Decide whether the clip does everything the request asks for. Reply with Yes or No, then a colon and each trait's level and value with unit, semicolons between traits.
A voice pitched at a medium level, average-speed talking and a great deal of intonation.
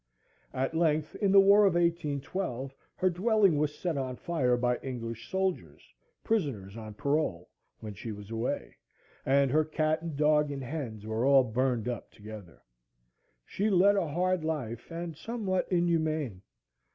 Yes: medium, 150 Hz; average, 150 wpm; wide, 6.1 semitones